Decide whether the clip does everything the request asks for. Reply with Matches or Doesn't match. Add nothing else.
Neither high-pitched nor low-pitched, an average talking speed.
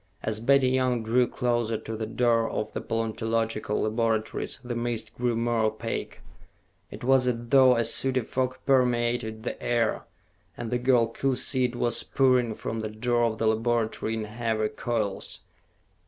Doesn't match